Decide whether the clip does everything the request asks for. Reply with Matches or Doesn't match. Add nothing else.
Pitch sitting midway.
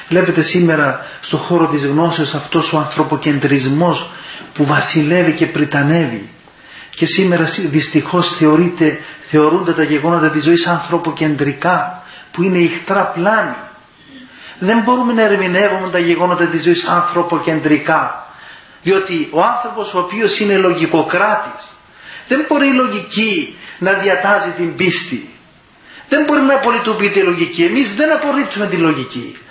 Matches